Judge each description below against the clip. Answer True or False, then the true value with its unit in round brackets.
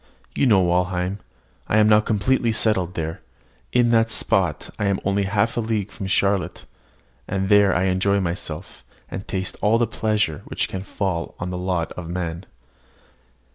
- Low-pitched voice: True (95 Hz)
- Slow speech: False (170 wpm)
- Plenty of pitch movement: False (2.8 semitones)